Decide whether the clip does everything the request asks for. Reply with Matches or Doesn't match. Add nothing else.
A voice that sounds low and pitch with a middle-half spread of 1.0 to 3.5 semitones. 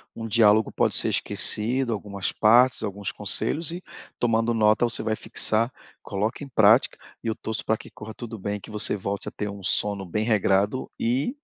Matches